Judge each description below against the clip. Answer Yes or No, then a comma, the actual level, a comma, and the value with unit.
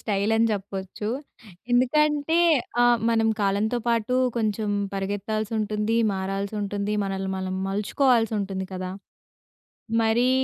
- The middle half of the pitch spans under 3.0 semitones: Yes, narrow, 2.6 semitones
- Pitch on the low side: No, high, 210 Hz